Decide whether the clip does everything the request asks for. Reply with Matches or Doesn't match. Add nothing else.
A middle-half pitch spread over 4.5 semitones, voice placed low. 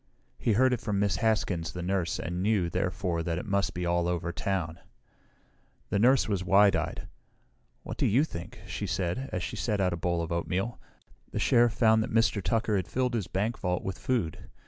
Doesn't match